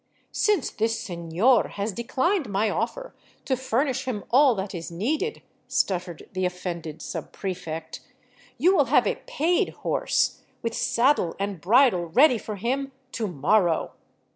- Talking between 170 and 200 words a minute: No, average, 150 wpm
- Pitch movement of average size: No, wide, 6.6 semitones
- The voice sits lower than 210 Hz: No, high, 220 Hz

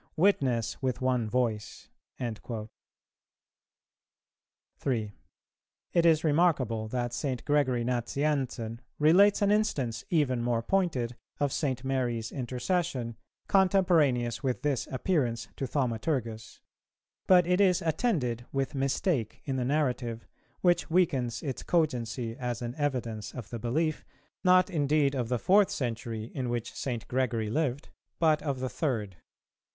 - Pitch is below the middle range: Yes, low, 130 Hz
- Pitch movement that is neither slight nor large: Yes, average, 4.8 semitones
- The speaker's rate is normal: No, slow, 125 wpm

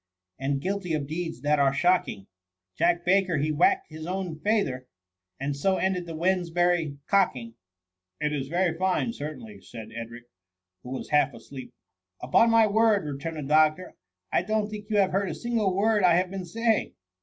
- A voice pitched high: No, medium, 170 Hz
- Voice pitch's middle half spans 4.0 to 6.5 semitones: Yes, wide, 5.5 semitones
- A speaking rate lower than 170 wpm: No, average, 190 wpm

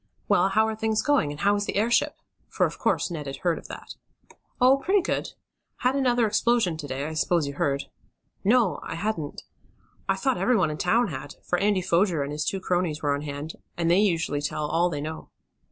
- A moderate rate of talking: No, fast, 215 wpm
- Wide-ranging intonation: Yes, wide, 6.5 semitones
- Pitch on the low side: No, medium, 175 Hz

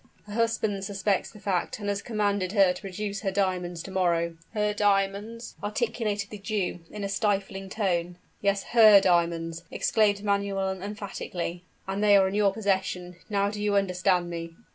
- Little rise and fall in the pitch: Yes, narrow, 2.1 semitones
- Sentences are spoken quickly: No, average, 170 wpm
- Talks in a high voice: Yes, high, 200 Hz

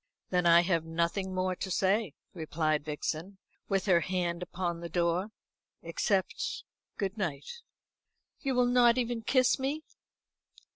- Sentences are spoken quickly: No, slow, 135 wpm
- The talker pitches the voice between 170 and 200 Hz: Yes, medium, 185 Hz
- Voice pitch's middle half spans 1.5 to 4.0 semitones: No, average, 5.1 semitones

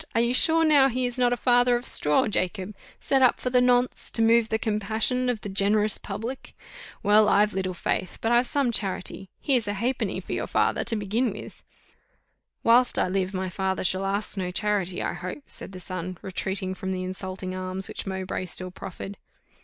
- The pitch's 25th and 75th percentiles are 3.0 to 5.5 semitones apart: Yes, average, 4.4 semitones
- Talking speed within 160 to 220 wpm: Yes, average, 200 wpm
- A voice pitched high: Yes, high, 210 Hz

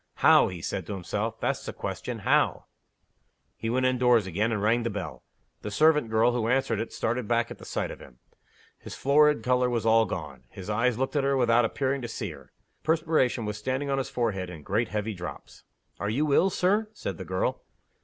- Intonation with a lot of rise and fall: No, average, 4.0 semitones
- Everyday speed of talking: No, fast, 215 wpm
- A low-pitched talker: Yes, low, 115 Hz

